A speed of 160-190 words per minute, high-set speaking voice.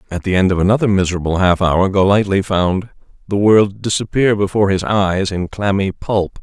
No: average, 180 wpm; low, 100 Hz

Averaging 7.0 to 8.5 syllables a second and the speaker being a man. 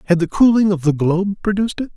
Yes: 7.1 syllables/s; male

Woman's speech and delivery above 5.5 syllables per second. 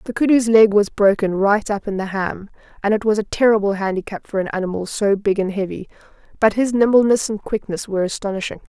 Yes: female; 6.0 syllables/s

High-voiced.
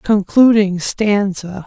Yes: high, 200 Hz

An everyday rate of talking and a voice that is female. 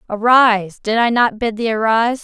Yes: average, 190 wpm; female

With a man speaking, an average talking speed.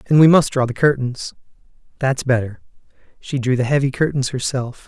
Yes: male; average, 160 wpm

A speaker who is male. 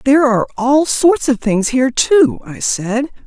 No: female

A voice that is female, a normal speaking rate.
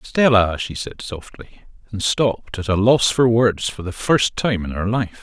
No: male; average, 195 wpm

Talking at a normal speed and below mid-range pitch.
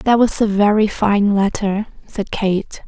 No: average, 165 wpm; high, 205 Hz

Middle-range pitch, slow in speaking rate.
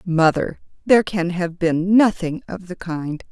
No: medium, 180 Hz; average, 165 wpm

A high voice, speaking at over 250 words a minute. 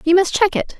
Yes: very high, 370 Hz; fast, 300 wpm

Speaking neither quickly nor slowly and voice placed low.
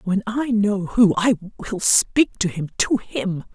No: average, 170 wpm; high, 205 Hz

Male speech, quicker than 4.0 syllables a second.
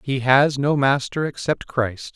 No: male; 3.9 syllables/s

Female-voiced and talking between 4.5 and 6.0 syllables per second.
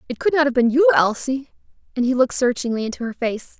No: female; 6.6 syllables/s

